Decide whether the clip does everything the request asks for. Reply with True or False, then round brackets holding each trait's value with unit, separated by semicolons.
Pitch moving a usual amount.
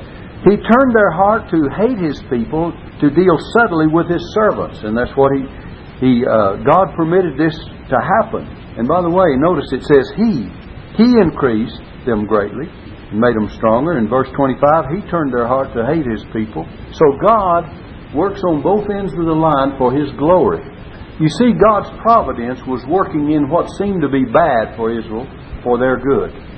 False (7.1 semitones)